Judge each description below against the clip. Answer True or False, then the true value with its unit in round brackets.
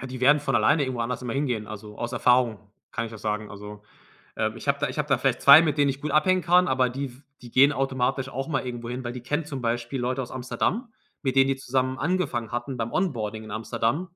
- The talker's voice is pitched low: True (130 Hz)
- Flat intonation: False (3.0 semitones)